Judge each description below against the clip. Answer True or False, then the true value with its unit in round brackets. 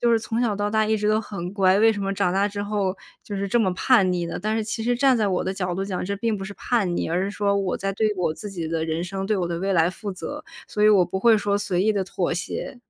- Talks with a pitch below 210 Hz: True (200 Hz)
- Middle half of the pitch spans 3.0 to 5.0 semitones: False (2.6 semitones)